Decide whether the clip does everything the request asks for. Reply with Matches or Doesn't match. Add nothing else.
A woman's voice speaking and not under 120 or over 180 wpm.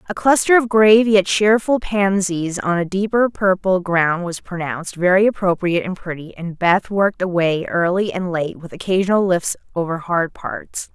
Matches